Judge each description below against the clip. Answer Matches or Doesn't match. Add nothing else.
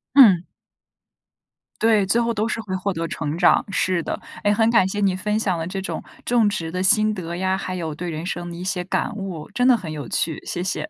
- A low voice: Doesn't match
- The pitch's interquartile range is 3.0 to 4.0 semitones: Matches